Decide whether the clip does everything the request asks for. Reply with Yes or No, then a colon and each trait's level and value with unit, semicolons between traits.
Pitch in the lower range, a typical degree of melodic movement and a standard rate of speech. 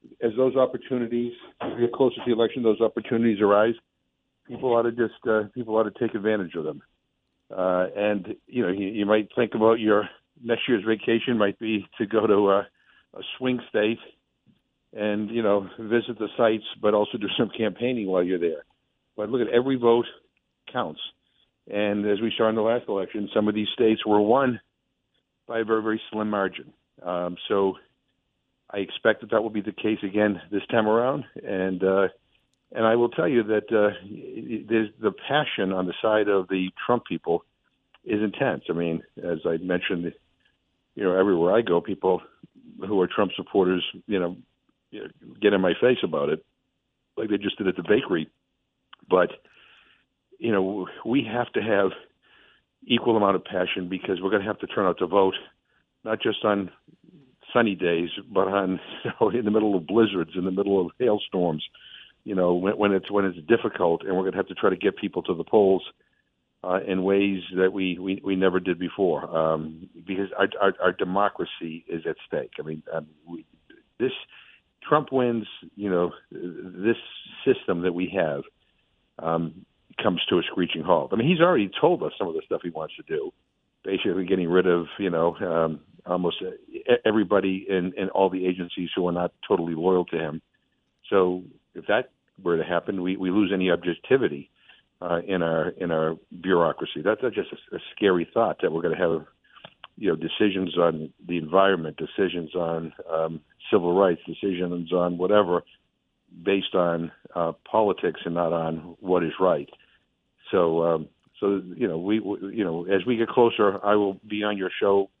Yes: low, 100 Hz; average, 3.7 semitones; average, 185 wpm